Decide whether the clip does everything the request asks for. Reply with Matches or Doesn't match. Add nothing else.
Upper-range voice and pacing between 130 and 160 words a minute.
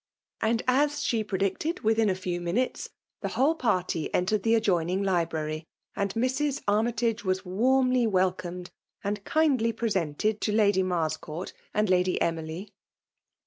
Matches